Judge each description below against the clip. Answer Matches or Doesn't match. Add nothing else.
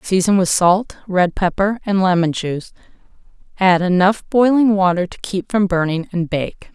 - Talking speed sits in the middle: Matches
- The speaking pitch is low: Doesn't match